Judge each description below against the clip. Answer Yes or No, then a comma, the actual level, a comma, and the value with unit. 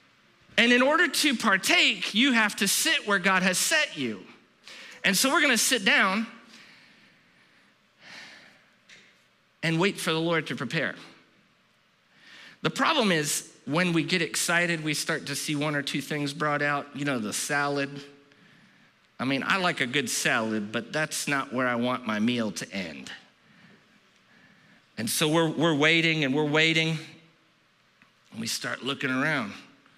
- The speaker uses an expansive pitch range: Yes, wide, 5.7 semitones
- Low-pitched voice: No, medium, 160 Hz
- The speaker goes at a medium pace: Yes, average, 155 wpm